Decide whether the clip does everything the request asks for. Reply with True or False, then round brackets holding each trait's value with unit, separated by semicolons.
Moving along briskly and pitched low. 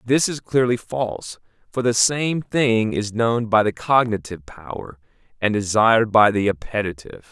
False (155 wpm; 110 Hz)